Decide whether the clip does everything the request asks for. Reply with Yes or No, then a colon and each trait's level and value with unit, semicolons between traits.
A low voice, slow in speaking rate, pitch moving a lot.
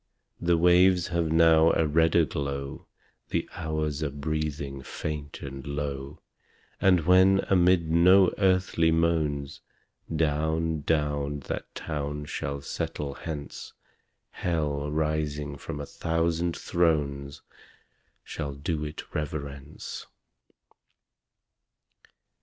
No: very low, 75 Hz; slow, 100 wpm; narrow, 2.5 semitones